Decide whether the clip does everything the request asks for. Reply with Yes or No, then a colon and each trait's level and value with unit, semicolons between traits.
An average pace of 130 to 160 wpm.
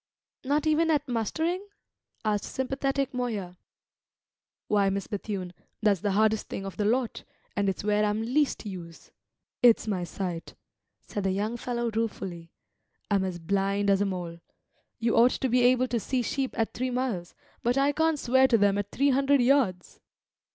No: average, 170 wpm